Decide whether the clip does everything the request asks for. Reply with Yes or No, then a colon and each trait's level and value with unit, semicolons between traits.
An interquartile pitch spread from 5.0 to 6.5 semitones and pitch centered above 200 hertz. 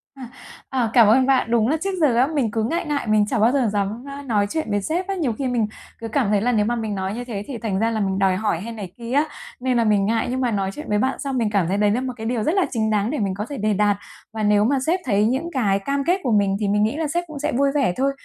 No: average, 4.6 semitones; high, 230 Hz